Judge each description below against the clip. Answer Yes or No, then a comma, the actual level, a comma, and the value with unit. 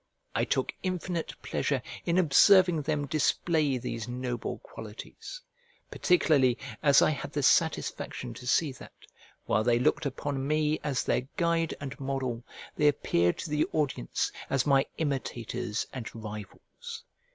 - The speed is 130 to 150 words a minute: Yes, average, 140 wpm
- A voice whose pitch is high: No, medium, 140 Hz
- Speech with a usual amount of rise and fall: Yes, average, 4.2 semitones